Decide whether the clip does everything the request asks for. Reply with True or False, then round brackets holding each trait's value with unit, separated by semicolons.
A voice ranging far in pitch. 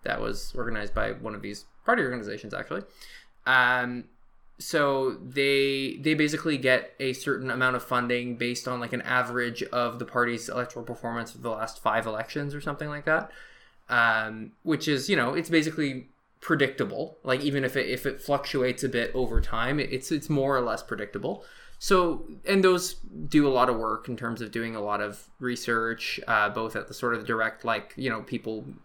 False (3.3 semitones)